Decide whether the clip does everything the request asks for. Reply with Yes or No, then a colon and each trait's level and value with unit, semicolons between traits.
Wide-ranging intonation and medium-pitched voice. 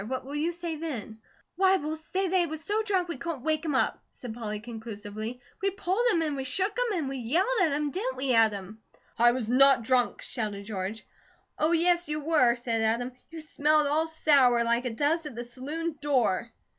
No: wide, 5.8 semitones; very high, 285 Hz